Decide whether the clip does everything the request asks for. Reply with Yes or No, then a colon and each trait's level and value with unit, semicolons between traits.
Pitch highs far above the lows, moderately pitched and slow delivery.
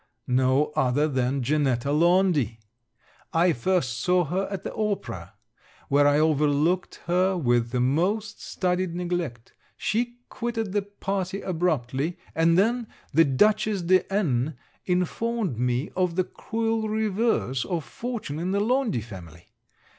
Yes: wide, 6.6 semitones; medium, 175 Hz; slow, 130 wpm